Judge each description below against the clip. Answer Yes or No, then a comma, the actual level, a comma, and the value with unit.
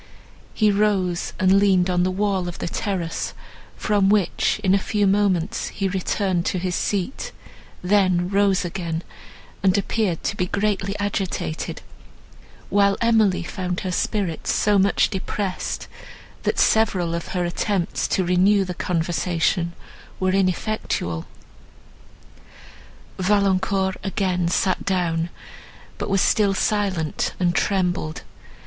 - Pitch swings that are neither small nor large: No, narrow, 2.1 semitones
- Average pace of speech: No, slow, 125 wpm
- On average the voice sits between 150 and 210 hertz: Yes, high, 190 Hz